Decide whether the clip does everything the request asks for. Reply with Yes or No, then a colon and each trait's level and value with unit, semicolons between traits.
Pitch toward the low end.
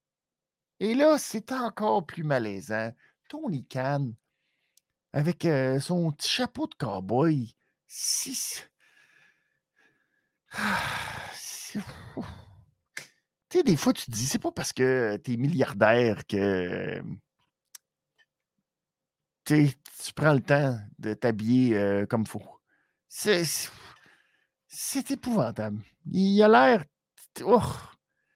No: medium, 150 Hz